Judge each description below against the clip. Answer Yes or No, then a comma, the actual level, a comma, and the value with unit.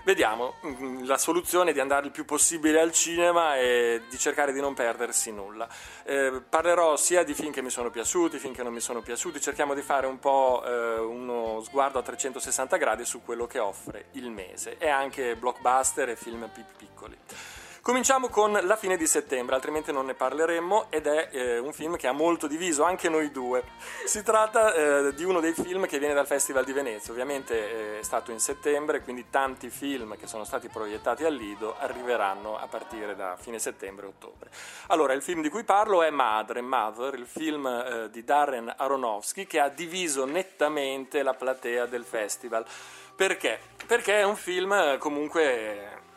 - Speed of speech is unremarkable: No, fast, 185 wpm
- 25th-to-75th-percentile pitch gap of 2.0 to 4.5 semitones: No, average, 5.2 semitones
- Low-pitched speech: No, medium, 145 Hz